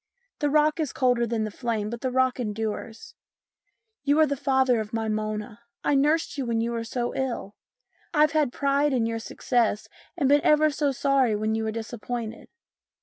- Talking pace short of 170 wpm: No, average, 190 wpm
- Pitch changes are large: No, average, 4.0 semitones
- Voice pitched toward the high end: Yes, high, 245 Hz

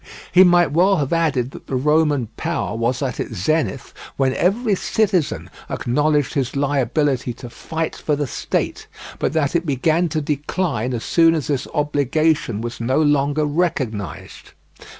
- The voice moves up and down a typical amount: Yes, average, 3.8 semitones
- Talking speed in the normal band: Yes, average, 155 wpm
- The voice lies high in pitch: No, medium, 145 Hz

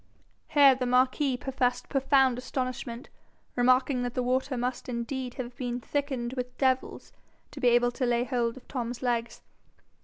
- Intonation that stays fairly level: Yes, narrow, 1.4 semitones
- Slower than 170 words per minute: Yes, average, 155 wpm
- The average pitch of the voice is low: No, very high, 250 Hz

